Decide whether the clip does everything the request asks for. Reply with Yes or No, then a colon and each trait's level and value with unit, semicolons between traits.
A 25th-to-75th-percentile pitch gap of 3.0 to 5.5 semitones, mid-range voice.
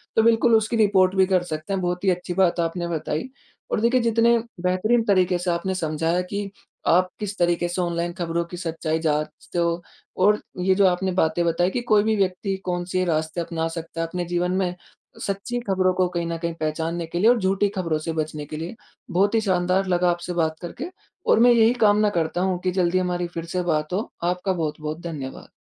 No: narrow, 2.5 semitones; medium, 180 Hz